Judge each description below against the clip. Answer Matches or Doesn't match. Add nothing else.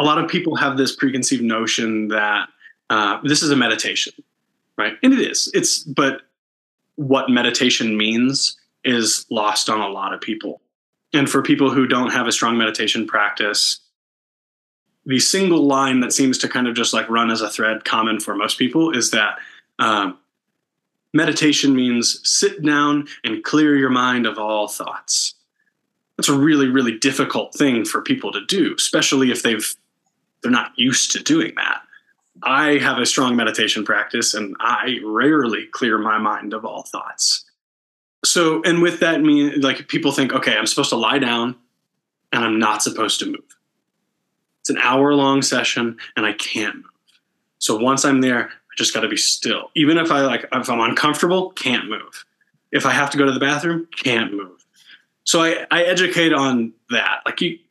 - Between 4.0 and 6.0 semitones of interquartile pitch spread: Matches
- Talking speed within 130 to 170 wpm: Doesn't match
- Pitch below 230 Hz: Matches